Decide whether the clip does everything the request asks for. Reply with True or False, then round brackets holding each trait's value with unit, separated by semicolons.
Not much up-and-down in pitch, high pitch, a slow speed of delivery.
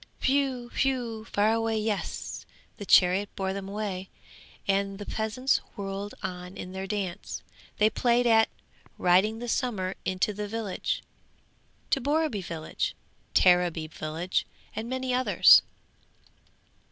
False (3.7 semitones; 205 Hz; 125 wpm)